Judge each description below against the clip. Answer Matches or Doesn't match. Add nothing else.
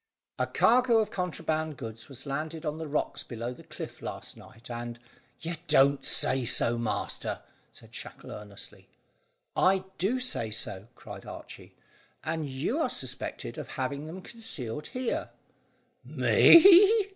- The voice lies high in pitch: Doesn't match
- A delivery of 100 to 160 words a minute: Matches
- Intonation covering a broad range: Matches